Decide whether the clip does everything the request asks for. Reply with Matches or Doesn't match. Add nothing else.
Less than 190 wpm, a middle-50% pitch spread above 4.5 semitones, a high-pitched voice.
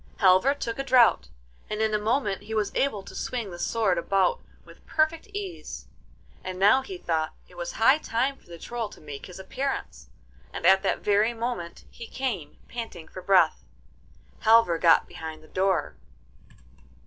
Matches